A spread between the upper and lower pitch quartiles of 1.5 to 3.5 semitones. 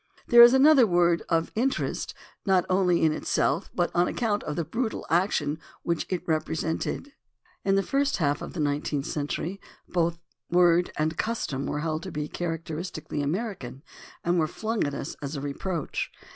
No: average, 4.2 semitones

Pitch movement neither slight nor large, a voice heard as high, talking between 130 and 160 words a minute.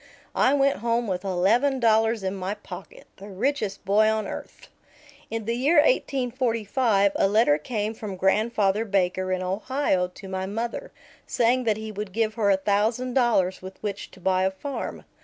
No: average, 3.8 semitones; high, 215 Hz; average, 175 wpm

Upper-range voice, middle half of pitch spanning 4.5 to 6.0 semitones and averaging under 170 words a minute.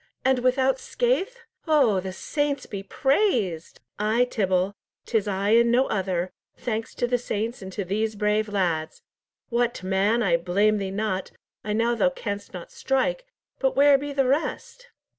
Yes: high, 220 Hz; average, 5.2 semitones; average, 160 wpm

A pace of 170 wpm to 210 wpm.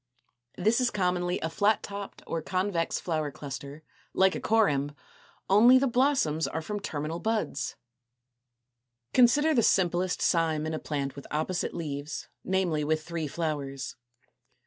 No: average, 150 wpm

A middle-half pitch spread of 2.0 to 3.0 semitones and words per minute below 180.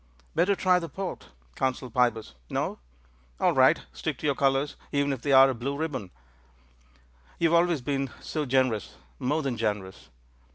No: average, 3.7 semitones; average, 165 wpm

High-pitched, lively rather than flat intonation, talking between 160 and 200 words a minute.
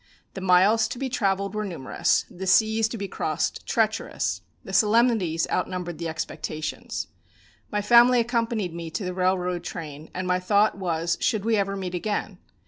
No: high, 195 Hz; average, 3.6 semitones; average, 165 wpm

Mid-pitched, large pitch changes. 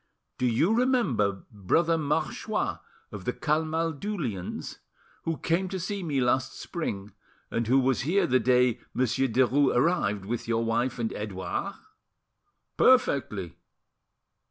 No: low, 130 Hz; wide, 6.4 semitones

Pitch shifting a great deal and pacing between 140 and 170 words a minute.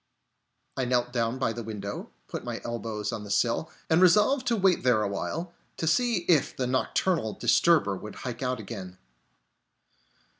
Yes: wide, 7.3 semitones; average, 160 wpm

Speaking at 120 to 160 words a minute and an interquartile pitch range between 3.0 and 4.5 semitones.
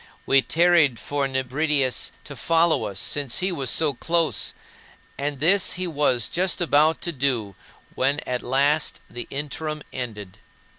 Yes: average, 145 wpm; average, 3.8 semitones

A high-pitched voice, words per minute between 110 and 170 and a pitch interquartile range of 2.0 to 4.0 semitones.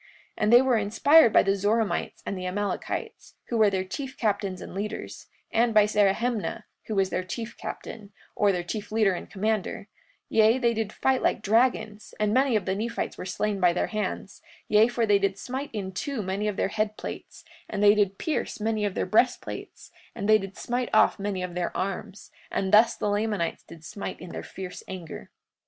No: high, 210 Hz; fast, 205 wpm; narrow, 2.5 semitones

